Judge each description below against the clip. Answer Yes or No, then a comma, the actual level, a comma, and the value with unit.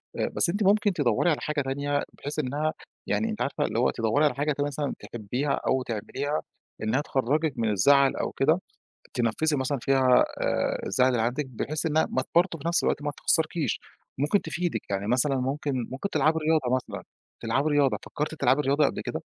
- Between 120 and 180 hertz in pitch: Yes, medium, 140 Hz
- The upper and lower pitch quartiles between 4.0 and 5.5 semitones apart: No, average, 3.2 semitones